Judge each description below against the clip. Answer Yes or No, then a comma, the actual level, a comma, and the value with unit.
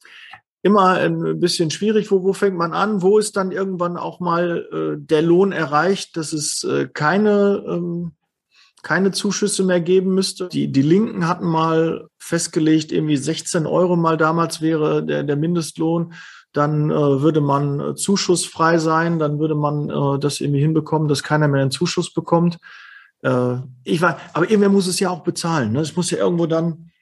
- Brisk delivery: No, average, 180 wpm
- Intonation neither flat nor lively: Yes, average, 3.0 semitones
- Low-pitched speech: No, medium, 170 Hz